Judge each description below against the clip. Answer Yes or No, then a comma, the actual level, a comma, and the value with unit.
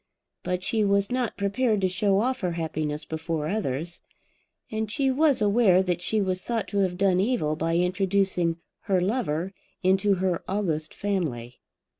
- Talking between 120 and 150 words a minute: No, average, 160 wpm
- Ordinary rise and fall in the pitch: Yes, average, 3.7 semitones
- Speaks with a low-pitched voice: No, high, 190 Hz